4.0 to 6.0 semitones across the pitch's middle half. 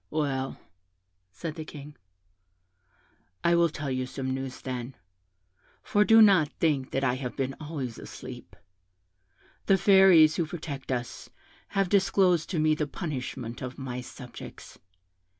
Yes: average, 4.5 semitones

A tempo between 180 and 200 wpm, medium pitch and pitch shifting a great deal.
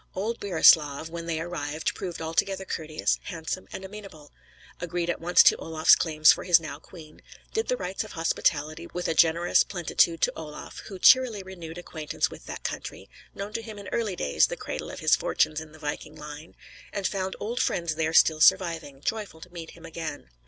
No: average, 195 wpm; medium, 165 Hz; average, 3.2 semitones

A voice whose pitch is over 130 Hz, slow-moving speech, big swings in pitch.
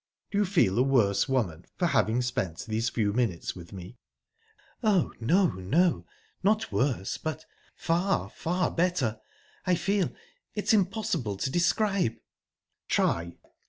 Yes: medium, 140 Hz; slow, 125 wpm; wide, 9.0 semitones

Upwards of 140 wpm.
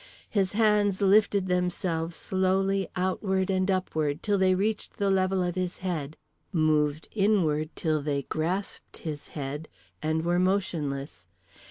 No: slow, 135 wpm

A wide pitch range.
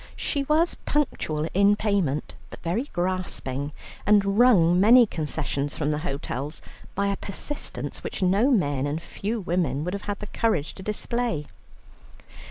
Yes: wide, 5.9 semitones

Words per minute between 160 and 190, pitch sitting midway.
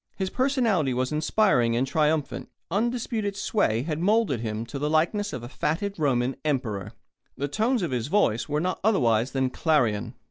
Yes: average, 170 wpm; medium, 150 Hz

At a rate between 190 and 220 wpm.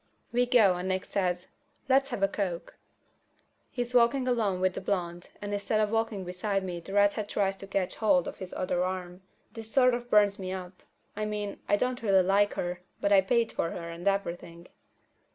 Yes: fast, 205 wpm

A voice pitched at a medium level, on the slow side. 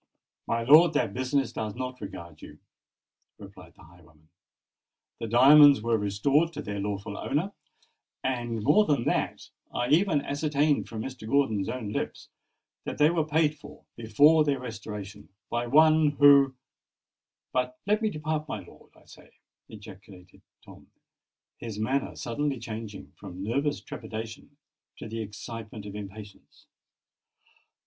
No: low, 120 Hz; slow, 130 wpm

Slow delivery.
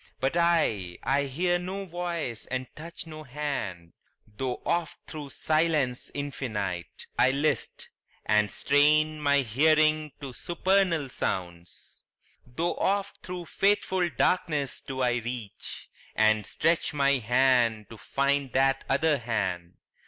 Yes: slow, 125 wpm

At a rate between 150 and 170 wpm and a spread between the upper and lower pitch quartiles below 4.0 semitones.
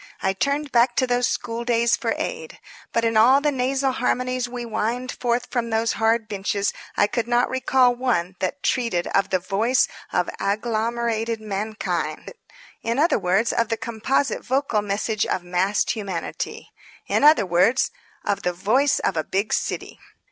Yes: average, 165 wpm; average, 3.5 semitones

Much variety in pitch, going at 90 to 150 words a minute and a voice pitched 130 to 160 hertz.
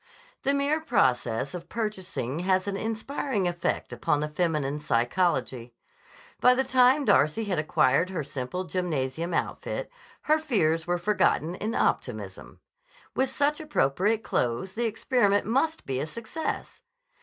No: wide, 7.8 semitones; slow, 135 wpm; medium, 185 Hz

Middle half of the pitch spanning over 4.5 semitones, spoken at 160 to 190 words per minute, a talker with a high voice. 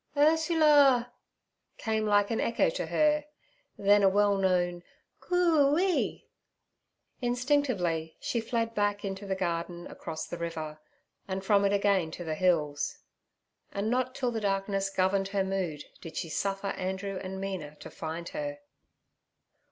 No: average, 5.1 semitones; average, 145 wpm; high, 195 Hz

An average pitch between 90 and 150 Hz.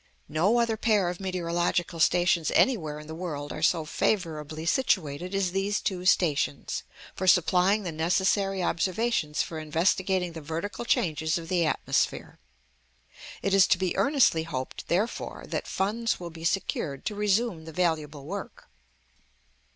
No: medium, 175 Hz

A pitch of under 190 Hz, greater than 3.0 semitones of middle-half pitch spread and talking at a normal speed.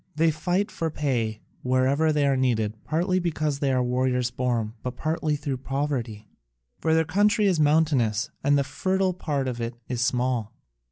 Yes: medium, 140 Hz; average, 4.3 semitones; average, 165 wpm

